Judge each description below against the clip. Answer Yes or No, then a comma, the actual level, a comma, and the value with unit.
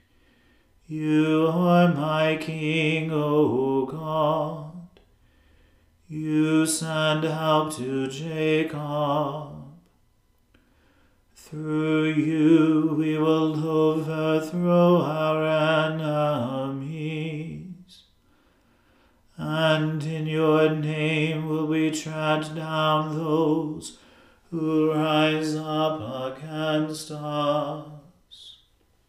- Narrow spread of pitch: Yes, narrow, 0.6 semitones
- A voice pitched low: No, medium, 155 Hz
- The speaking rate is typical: No, slow, 65 wpm